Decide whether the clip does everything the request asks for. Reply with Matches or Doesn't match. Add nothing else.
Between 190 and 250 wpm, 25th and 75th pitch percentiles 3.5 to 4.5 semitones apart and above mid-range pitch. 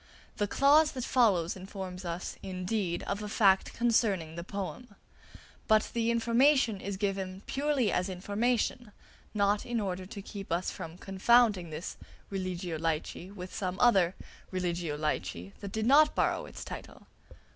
Doesn't match